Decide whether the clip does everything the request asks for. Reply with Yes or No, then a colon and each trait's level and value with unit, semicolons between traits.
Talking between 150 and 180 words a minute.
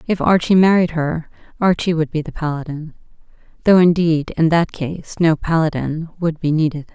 Yes: average, 165 wpm